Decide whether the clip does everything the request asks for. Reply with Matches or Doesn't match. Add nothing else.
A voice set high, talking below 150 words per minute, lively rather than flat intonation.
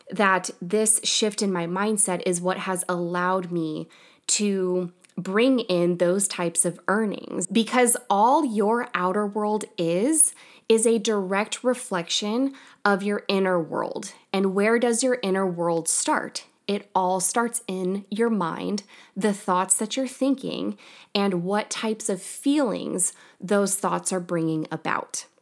Doesn't match